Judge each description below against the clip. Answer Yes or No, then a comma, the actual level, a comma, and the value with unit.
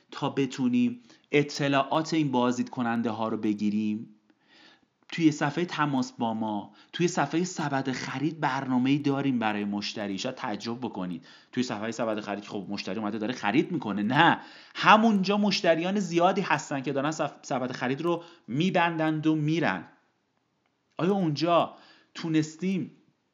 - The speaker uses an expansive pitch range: Yes, wide, 6.2 semitones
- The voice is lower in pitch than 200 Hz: Yes, medium, 140 Hz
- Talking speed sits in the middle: Yes, average, 130 wpm